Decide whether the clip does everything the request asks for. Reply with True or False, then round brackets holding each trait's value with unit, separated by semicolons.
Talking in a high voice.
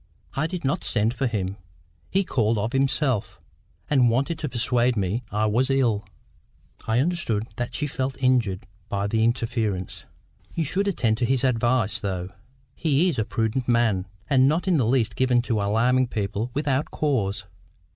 False (120 Hz)